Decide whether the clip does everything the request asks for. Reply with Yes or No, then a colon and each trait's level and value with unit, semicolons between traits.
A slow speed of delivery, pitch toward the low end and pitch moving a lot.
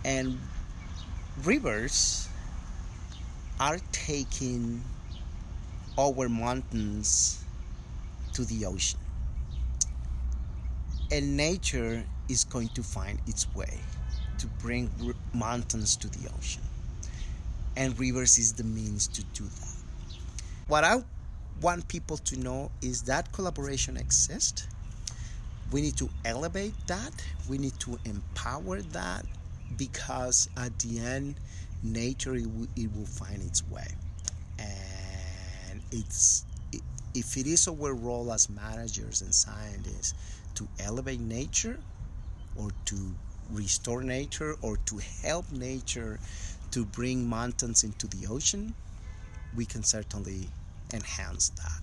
Yes: slow, 110 wpm; low, 100 Hz; wide, 5.9 semitones